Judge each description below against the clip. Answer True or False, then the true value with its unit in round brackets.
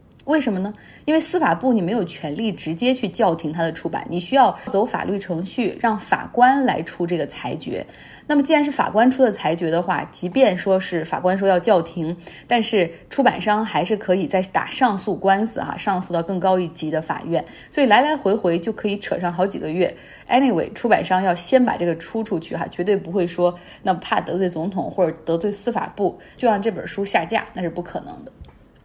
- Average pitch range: True (4.5 semitones)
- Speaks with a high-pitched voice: True (195 Hz)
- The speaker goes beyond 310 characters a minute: True (320 characters per minute)